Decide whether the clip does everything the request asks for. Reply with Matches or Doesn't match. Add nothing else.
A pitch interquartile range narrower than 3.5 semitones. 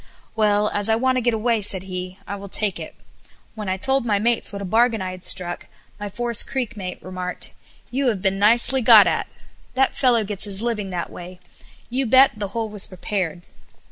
Doesn't match